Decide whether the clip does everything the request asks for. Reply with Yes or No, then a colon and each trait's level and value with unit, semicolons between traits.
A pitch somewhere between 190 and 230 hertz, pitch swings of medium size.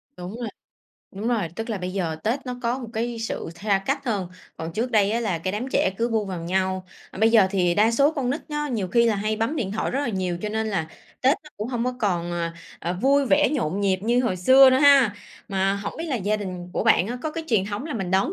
Yes: high, 215 Hz; average, 4.6 semitones